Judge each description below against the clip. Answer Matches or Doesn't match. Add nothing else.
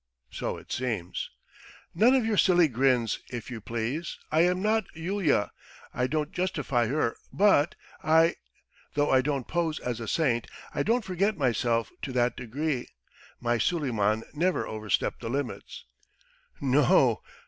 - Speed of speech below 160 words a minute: Matches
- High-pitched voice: Doesn't match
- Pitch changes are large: Matches